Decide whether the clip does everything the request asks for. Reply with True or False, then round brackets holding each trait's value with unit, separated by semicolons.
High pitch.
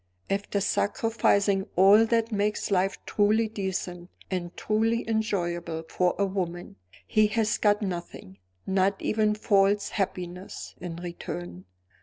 True (195 Hz)